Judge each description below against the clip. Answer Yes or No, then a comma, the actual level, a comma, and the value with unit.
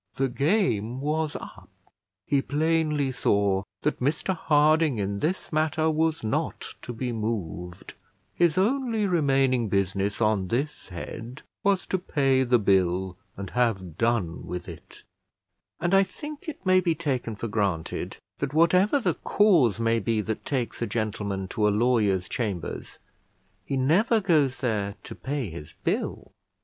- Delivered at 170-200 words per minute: No, average, 150 wpm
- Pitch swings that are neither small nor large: No, wide, 7.6 semitones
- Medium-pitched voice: No, low, 125 Hz